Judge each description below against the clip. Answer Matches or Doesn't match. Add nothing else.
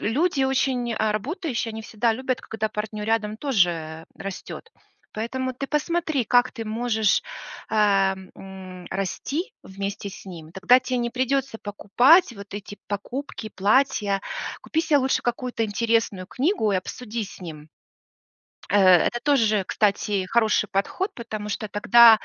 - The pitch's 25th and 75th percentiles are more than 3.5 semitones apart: Matches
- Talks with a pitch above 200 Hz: Matches